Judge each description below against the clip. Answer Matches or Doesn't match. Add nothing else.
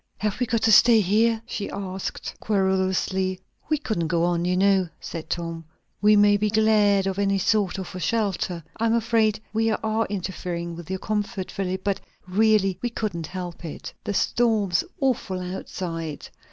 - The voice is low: Doesn't match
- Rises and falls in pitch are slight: Doesn't match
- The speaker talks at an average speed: Matches